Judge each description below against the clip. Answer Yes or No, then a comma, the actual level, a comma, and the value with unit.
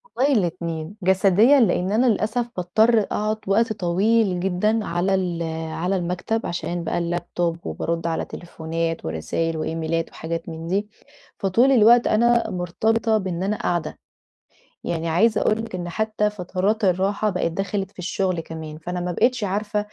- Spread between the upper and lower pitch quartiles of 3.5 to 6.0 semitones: Yes, average, 4.0 semitones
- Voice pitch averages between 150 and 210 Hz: Yes, medium, 185 Hz